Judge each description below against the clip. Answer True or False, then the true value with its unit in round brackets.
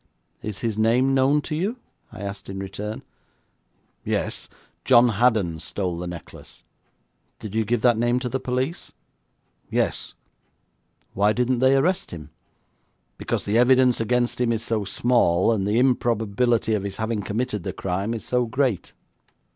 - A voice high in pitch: False (115 Hz)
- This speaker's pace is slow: False (155 wpm)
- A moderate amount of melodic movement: True (3.6 semitones)